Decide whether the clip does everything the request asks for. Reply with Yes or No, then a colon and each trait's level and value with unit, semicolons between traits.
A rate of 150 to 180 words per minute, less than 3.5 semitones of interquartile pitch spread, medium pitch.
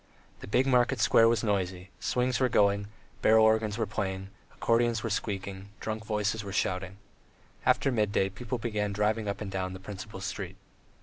No: average, 170 wpm; narrow, 2.5 semitones; low, 105 Hz